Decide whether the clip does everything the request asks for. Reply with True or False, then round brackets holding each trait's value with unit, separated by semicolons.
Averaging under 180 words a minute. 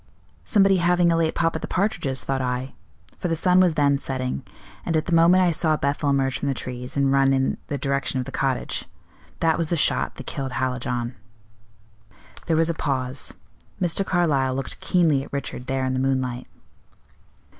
False (190 wpm)